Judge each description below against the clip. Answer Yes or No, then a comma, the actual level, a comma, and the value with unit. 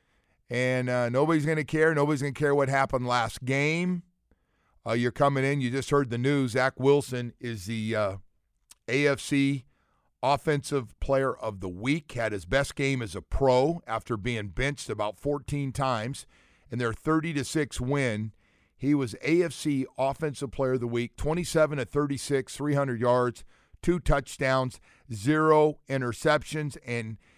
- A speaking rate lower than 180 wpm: Yes, average, 150 wpm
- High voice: No, low, 135 Hz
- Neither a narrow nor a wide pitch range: Yes, average, 3.3 semitones